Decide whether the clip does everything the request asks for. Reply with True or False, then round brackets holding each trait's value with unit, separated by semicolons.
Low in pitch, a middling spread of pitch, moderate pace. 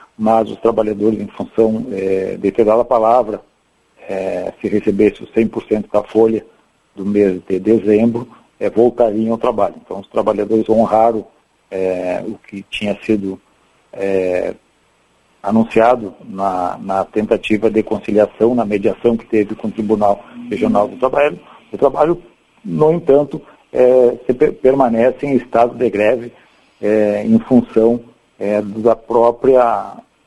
False (110 Hz; 2.0 semitones; 135 wpm)